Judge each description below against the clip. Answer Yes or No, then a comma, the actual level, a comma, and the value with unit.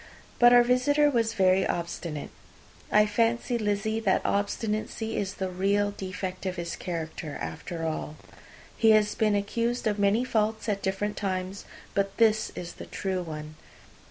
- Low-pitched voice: No, high, 205 Hz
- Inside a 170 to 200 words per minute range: No, average, 155 wpm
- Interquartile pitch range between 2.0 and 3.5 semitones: Yes, average, 3.1 semitones